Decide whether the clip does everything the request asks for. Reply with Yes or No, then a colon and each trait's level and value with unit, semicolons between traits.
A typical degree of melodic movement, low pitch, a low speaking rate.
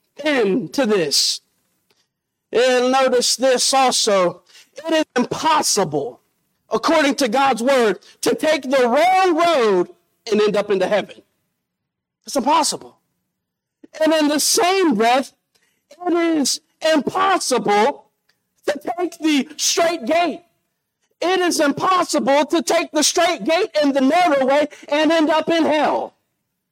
No: average, 4.3 semitones; very high, 300 Hz; slow, 125 wpm